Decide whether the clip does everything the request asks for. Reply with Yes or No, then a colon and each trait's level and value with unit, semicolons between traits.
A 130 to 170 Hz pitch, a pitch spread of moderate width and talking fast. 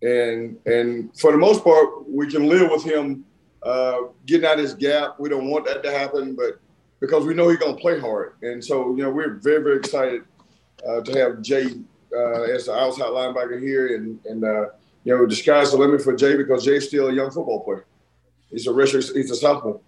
Yes: low, 135 Hz; average, 3.2 semitones; fast, 225 wpm